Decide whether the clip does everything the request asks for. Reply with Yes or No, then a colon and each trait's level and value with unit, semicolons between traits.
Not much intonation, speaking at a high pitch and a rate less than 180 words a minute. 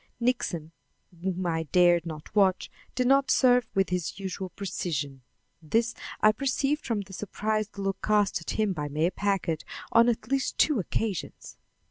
No: average, 4.6 semitones; high, 195 Hz; average, 155 wpm